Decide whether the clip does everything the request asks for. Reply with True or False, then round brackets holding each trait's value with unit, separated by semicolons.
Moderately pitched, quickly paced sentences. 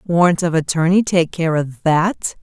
False (170 Hz; 150 wpm)